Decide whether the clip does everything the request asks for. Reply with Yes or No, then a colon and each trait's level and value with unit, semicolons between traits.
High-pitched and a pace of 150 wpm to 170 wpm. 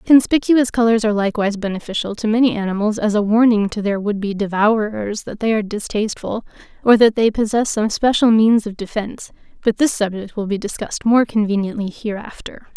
No: high, 215 Hz; average, 180 wpm